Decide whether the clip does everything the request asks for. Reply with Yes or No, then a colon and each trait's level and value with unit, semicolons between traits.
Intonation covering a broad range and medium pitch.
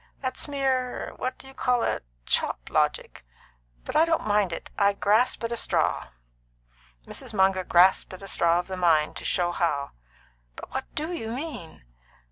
No: wide, 6.7 semitones; high, 205 Hz